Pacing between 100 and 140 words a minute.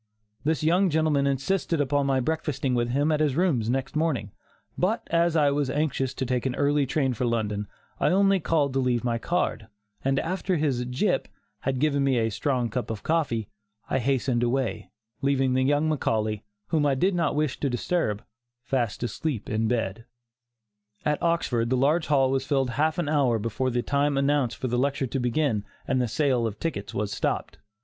No: average, 190 wpm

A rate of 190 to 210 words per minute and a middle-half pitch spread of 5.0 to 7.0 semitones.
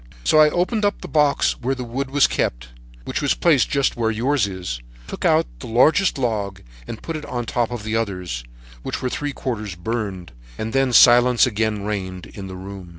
Yes: average, 200 wpm; wide, 5.4 semitones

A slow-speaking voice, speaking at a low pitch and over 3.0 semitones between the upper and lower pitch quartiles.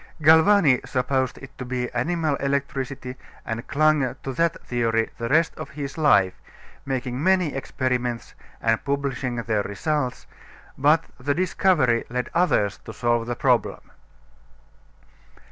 Yes: slow, 130 wpm; low, 130 Hz; average, 3.9 semitones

